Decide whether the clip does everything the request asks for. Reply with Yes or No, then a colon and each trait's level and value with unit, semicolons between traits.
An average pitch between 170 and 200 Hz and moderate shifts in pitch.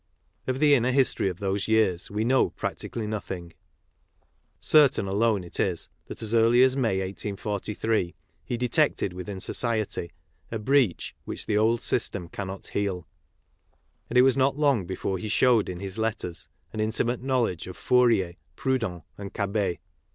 No: low, 110 Hz; average, 4.3 semitones